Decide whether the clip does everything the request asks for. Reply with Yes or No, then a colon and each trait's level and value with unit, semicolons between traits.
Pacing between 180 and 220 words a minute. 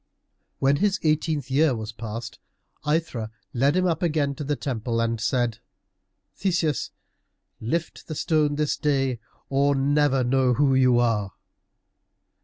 No: slow, 135 wpm